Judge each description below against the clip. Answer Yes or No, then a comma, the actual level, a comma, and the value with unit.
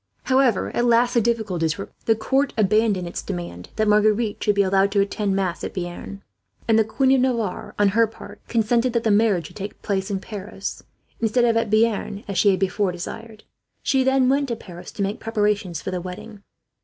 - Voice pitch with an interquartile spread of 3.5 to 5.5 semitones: No, average, 3.0 semitones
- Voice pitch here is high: Yes, high, 210 Hz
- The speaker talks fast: Yes, fast, 210 wpm